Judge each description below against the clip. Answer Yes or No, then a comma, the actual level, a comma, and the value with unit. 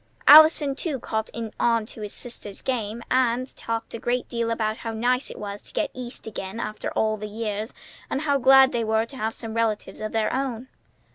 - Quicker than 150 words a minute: Yes, fast, 205 wpm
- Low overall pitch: No, high, 230 Hz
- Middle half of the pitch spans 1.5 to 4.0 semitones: Yes, average, 2.7 semitones